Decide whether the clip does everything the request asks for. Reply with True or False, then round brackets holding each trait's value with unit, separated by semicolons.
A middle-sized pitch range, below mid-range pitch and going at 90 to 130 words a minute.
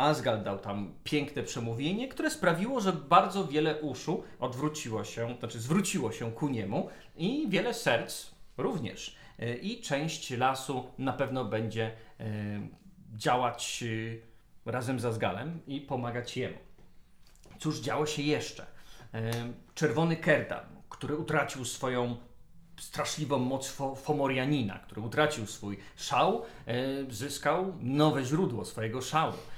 True (4.7 semitones; 130 Hz; 115 wpm)